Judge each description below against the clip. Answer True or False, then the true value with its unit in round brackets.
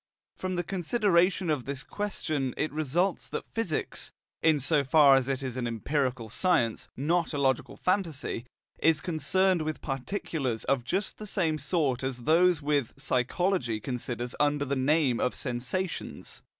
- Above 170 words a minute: False (150 wpm)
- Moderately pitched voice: True (145 Hz)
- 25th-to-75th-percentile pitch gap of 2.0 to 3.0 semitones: False (5.3 semitones)